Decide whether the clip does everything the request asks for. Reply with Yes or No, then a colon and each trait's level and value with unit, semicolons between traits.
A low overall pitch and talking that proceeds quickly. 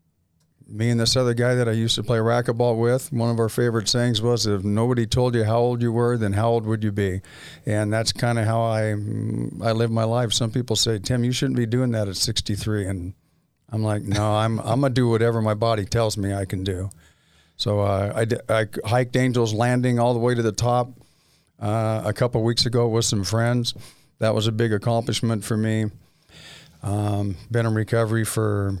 Yes: low, 115 Hz; fast, 220 wpm